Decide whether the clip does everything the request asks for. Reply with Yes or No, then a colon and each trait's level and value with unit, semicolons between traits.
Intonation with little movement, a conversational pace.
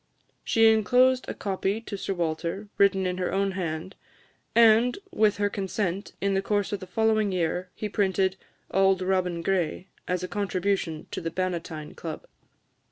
Yes: narrow, 2.2 semitones; average, 165 wpm